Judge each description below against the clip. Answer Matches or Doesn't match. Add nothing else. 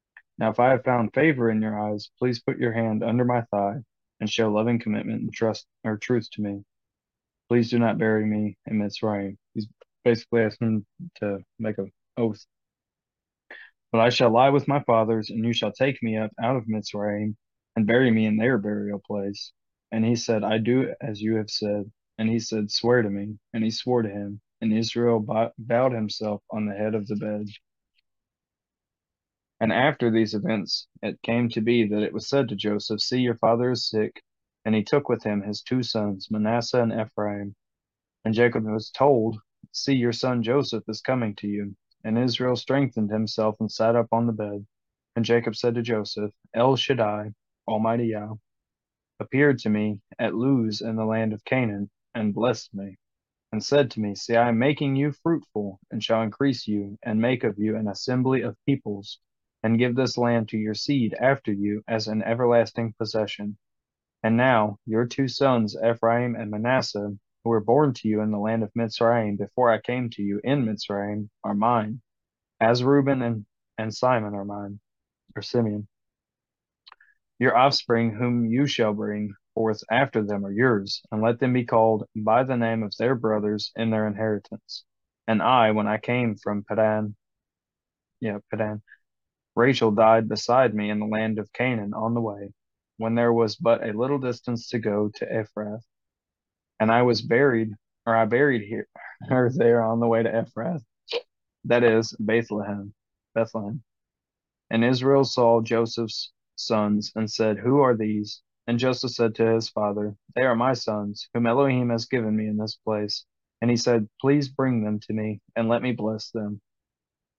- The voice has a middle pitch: Doesn't match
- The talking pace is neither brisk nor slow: Matches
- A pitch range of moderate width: Doesn't match